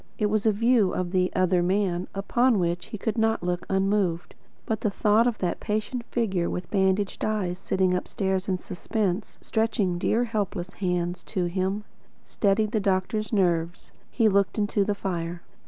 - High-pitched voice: Yes, high, 195 Hz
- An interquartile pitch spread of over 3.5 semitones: No, average, 2.9 semitones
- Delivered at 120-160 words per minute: No, average, 170 wpm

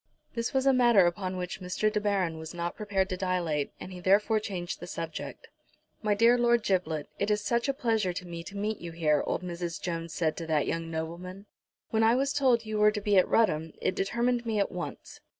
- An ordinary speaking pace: No, fast, 225 wpm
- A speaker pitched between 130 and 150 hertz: No, high, 190 Hz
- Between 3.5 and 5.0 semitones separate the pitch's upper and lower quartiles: Yes, average, 4.3 semitones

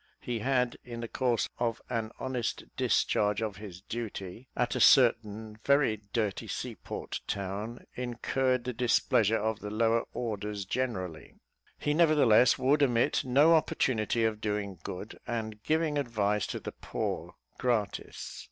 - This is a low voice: Yes, low, 115 Hz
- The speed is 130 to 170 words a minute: Yes, average, 145 wpm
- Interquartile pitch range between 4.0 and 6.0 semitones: No, average, 3.2 semitones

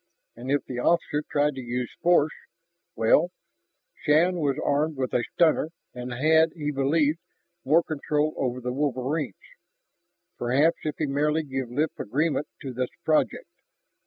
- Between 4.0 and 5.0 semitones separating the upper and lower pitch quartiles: No, average, 3.4 semitones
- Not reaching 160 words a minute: Yes, average, 145 wpm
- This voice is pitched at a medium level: Yes, medium, 145 Hz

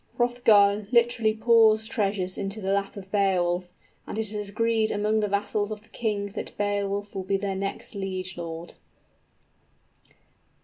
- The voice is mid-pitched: No, high, 205 Hz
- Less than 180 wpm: Yes, average, 145 wpm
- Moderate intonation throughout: No, narrow, 1.9 semitones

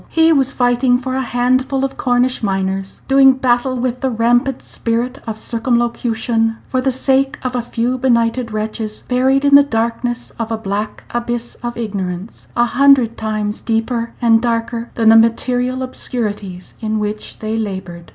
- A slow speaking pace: No, average, 160 wpm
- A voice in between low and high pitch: No, high, 240 Hz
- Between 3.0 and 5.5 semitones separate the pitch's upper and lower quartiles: No, narrow, 2.4 semitones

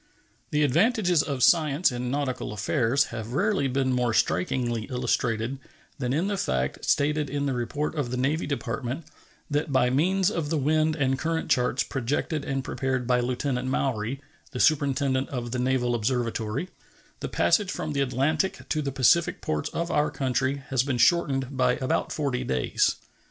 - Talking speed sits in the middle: Yes, average, 165 wpm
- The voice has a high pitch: No, low, 135 Hz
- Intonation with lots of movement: No, average, 3.3 semitones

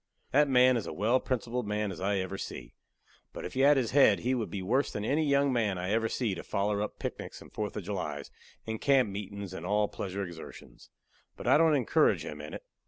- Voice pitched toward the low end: Yes, low, 105 Hz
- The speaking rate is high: Yes, fast, 235 wpm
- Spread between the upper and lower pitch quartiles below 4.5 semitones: No, average, 4.8 semitones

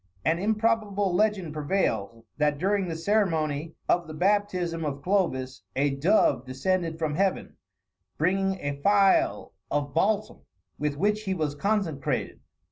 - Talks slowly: Yes, slow, 130 wpm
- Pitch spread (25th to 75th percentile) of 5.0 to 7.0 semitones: Yes, average, 5.3 semitones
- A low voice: No, medium, 170 Hz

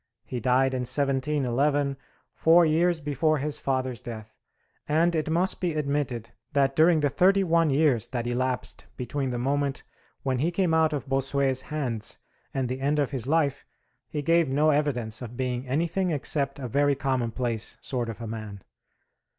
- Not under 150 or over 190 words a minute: Yes, average, 165 wpm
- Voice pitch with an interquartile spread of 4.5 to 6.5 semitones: No, average, 3.3 semitones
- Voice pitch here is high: No, medium, 140 Hz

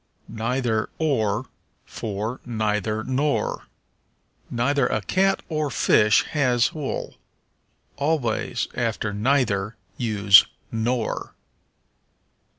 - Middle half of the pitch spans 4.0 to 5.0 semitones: Yes, average, 4.5 semitones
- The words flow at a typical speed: No, slow, 80 wpm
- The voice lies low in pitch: Yes, low, 120 Hz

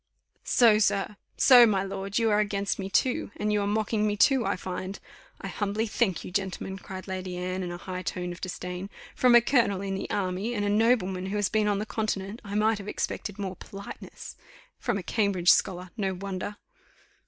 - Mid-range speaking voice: No, high, 200 Hz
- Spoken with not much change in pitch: Yes, narrow, 2.2 semitones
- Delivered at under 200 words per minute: No, fast, 205 wpm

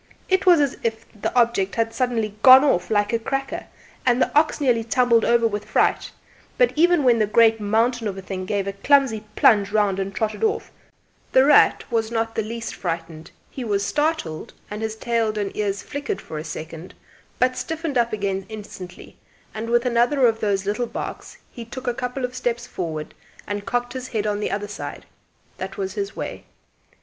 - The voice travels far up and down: No, average, 3.6 semitones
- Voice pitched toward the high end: Yes, high, 225 Hz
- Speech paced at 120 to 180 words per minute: No, average, 195 wpm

